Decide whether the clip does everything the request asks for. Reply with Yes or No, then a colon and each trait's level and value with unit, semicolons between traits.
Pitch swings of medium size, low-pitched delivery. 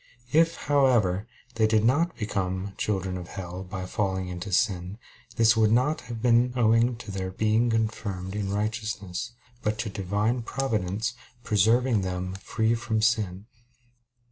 Yes: average, 3.6 semitones; low, 110 Hz